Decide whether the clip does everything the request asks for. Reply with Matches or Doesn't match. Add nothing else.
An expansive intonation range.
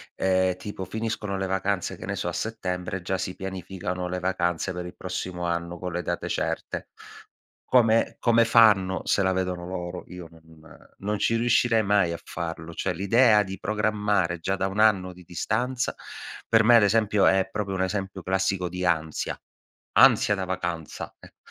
Doesn't match